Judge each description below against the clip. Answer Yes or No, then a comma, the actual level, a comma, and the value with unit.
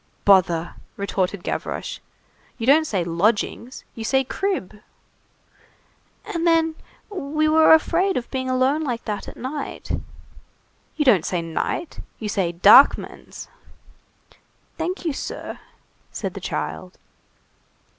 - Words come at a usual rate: No, slow, 115 wpm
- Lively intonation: Yes, wide, 8.0 semitones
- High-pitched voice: Yes, very high, 260 Hz